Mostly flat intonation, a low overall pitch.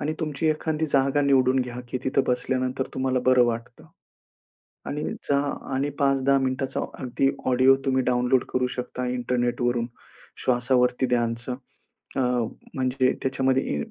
Yes: narrow, 1.5 semitones; low, 130 Hz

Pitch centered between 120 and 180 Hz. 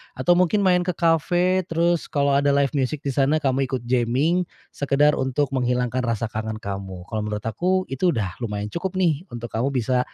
Yes: low, 135 Hz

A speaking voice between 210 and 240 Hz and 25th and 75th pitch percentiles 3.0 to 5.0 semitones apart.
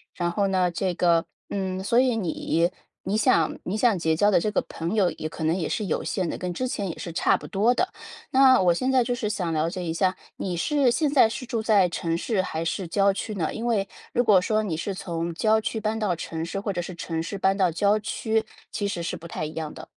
No: high, 190 Hz; average, 4.3 semitones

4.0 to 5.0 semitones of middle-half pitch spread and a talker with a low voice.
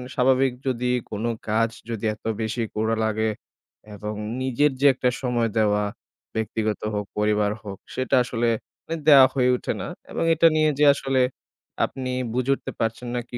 No: average, 3.2 semitones; low, 120 Hz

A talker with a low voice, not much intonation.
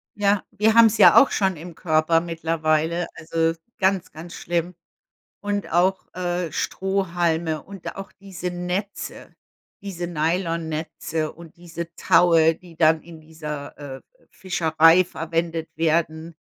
No: medium, 170 Hz; narrow, 2.1 semitones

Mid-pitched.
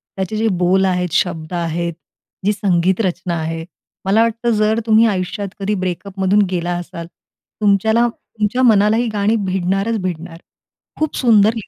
No: high, 195 Hz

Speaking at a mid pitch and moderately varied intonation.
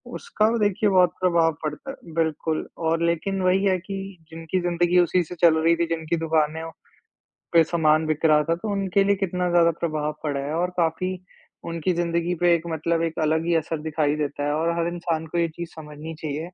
No: medium, 165 Hz; narrow, 2.0 semitones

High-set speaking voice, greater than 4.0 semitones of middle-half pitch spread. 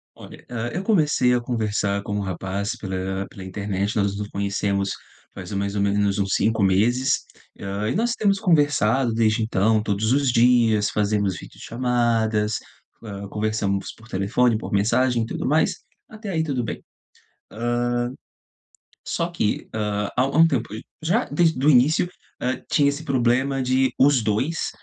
No: low, 110 Hz; average, 4.4 semitones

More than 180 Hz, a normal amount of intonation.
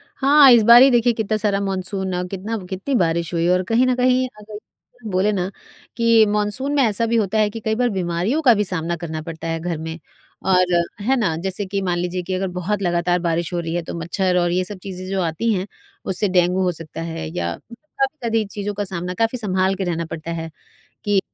Yes: high, 190 Hz; average, 4.2 semitones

